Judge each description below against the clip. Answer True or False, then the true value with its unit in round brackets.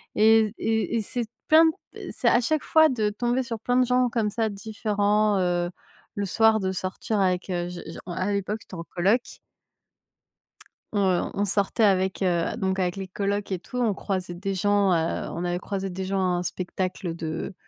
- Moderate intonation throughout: True (3.0 semitones)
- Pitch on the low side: False (200 Hz)